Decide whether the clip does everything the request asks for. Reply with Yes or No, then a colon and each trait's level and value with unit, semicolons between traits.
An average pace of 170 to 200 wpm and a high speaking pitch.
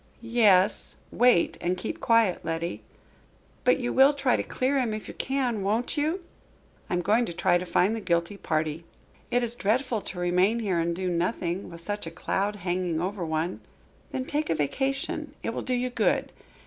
Yes: average, 190 wpm; high, 205 Hz